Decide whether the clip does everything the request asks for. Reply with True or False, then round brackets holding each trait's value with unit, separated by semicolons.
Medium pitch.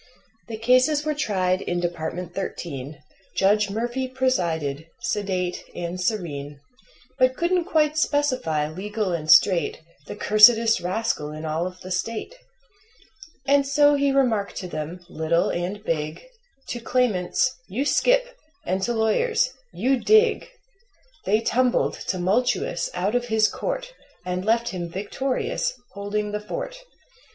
False (210 Hz)